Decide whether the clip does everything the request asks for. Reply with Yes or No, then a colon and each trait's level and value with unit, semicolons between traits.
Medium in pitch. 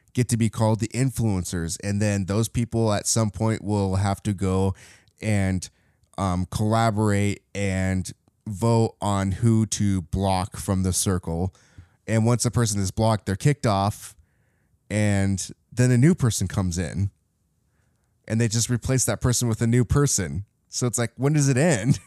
No: low, 105 Hz